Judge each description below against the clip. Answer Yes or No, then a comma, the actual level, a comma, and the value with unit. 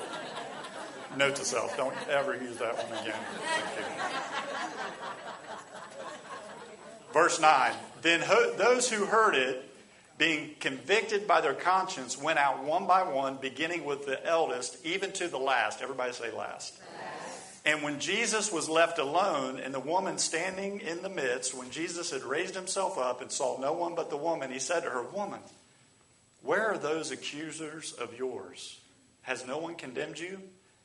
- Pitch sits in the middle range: Yes, medium, 165 Hz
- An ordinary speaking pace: Yes, average, 160 wpm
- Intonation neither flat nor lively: No, wide, 5.7 semitones